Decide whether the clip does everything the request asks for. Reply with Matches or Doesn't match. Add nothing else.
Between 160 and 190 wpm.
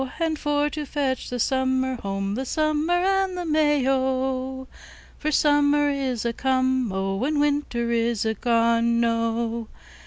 Doesn't match